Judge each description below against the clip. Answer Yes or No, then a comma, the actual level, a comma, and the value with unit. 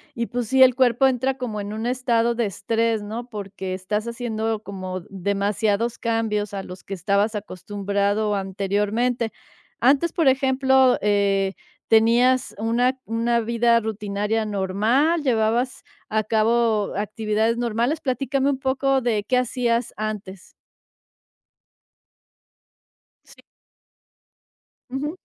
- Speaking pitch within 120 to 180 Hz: No, high, 225 Hz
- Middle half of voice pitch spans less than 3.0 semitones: No, average, 3.3 semitones